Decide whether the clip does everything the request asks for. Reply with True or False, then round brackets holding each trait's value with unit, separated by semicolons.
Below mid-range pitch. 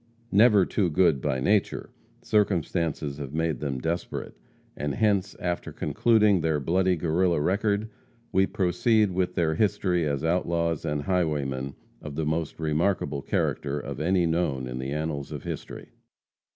True (85 Hz)